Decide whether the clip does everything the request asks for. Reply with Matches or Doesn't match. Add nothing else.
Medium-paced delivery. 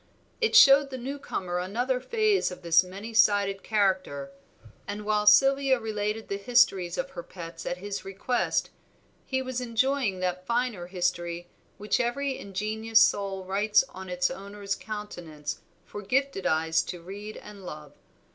Matches